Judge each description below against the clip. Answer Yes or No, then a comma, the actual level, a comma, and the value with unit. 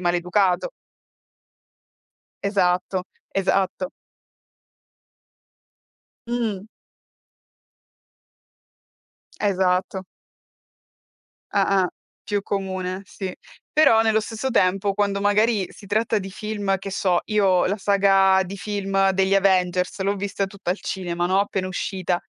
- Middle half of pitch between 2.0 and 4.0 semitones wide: No, narrow, 1.6 semitones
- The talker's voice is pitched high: Yes, high, 195 Hz